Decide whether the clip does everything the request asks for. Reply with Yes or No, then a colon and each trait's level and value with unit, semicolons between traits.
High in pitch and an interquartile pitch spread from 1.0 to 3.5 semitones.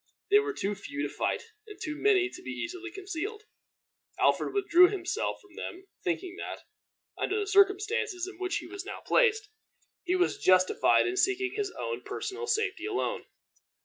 Yes: very high, 385 Hz; narrow, 2.4 semitones